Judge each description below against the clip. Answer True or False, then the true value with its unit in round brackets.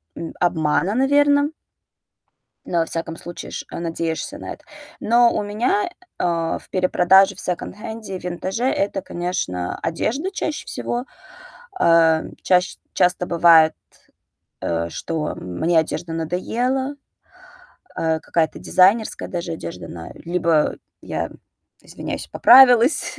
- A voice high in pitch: False (180 Hz)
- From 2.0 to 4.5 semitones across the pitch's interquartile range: False (5.5 semitones)